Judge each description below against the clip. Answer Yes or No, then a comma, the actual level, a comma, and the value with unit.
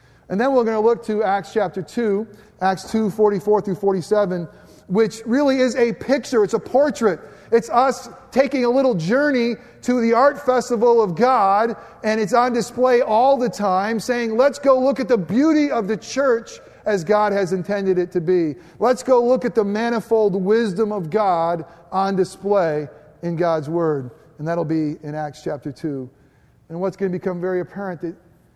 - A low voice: No, high, 210 Hz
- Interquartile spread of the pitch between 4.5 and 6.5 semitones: Yes, average, 5.2 semitones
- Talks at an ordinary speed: Yes, average, 185 wpm